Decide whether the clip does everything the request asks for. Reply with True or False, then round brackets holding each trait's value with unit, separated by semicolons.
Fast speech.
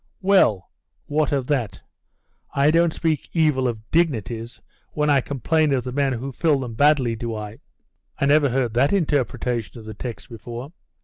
False (170 wpm)